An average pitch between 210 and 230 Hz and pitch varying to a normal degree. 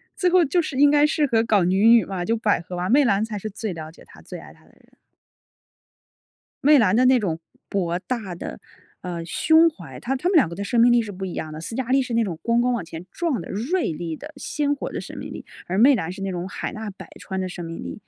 No: high, 215 Hz; wide, 6.7 semitones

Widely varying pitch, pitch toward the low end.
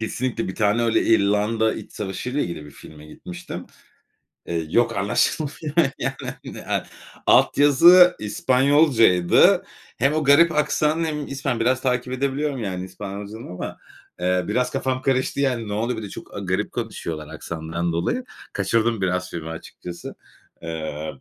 Yes: wide, 6.9 semitones; low, 115 Hz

